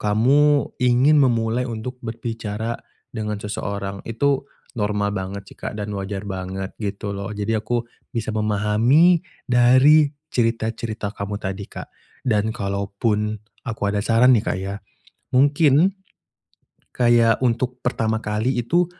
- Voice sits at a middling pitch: No, low, 110 Hz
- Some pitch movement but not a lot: Yes, average, 3.4 semitones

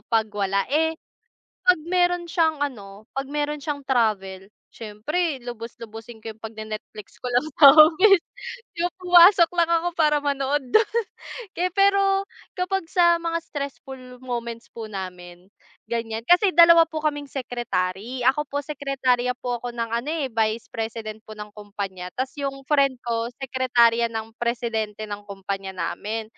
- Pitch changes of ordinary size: No, wide, 6.0 semitones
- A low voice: No, very high, 250 Hz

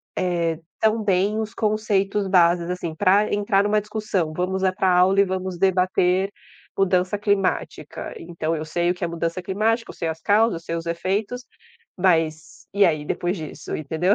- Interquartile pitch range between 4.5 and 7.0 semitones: No, average, 3.1 semitones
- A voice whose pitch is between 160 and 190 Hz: Yes, medium, 185 Hz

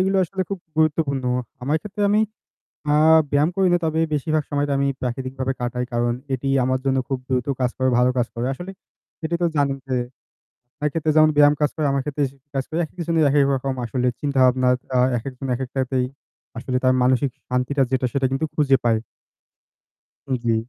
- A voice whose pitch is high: No, low, 135 Hz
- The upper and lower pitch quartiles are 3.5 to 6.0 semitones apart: No, average, 2.9 semitones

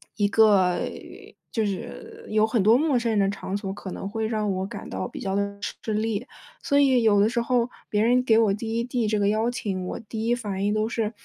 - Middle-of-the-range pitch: No, high, 220 Hz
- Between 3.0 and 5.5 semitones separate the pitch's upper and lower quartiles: No, narrow, 2.6 semitones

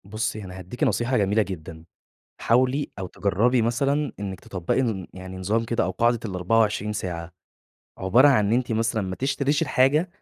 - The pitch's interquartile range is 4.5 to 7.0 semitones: Yes, average, 5.0 semitones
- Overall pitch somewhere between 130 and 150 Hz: No, low, 110 Hz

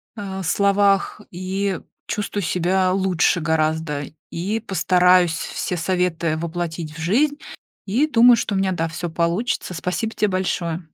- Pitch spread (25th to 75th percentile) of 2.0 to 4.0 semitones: Yes, average, 2.9 semitones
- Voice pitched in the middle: Yes, medium, 180 Hz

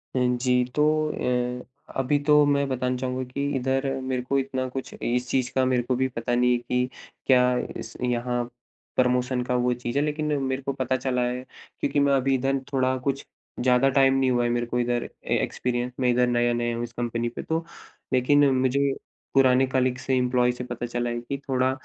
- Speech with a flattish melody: Yes, narrow, 1.4 semitones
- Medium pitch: No, low, 125 Hz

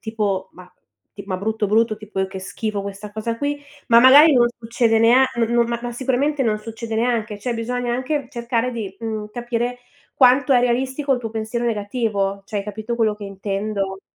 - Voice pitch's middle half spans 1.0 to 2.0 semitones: No, narrow, 2.6 semitones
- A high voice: Yes, high, 230 Hz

